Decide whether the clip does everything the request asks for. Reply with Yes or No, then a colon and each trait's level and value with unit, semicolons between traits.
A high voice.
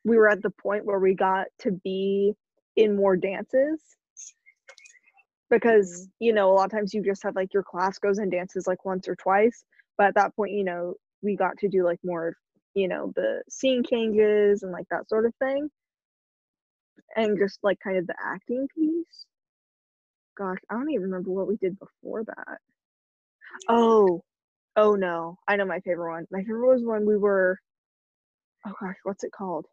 Yes: high, 200 Hz